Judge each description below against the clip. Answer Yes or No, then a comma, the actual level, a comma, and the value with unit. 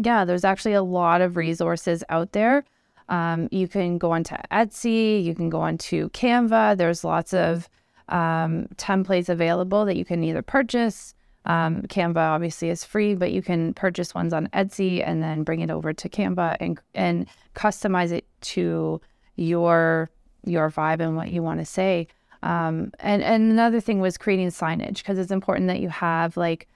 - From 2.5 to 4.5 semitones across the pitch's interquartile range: Yes, average, 3.1 semitones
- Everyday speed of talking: Yes, average, 175 wpm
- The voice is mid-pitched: Yes, medium, 175 Hz